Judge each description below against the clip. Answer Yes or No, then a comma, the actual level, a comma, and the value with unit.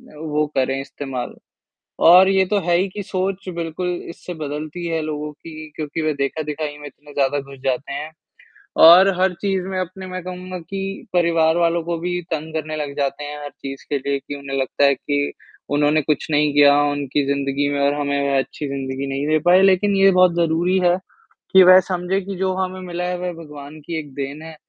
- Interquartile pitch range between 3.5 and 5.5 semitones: Yes, average, 4.1 semitones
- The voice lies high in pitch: No, medium, 155 Hz